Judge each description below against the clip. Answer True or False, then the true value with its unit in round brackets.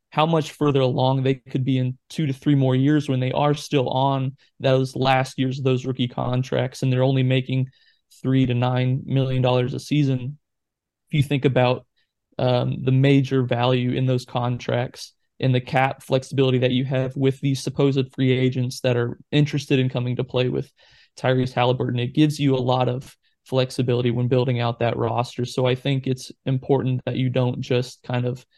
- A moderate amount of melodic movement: False (1.2 semitones)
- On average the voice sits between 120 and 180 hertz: True (130 Hz)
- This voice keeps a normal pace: True (195 wpm)